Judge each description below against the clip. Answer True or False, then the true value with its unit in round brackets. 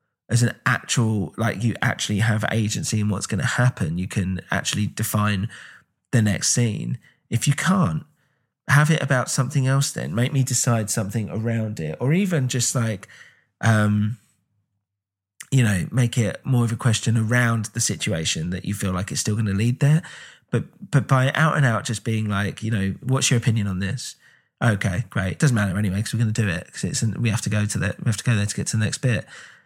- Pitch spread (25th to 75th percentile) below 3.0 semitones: False (3.7 semitones)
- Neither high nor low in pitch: False (115 Hz)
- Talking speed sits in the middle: False (215 wpm)